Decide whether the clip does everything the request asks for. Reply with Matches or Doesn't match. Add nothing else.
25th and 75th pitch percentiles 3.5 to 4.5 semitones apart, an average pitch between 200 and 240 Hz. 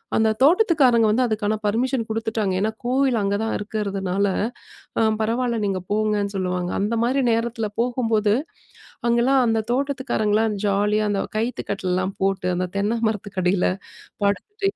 Doesn't match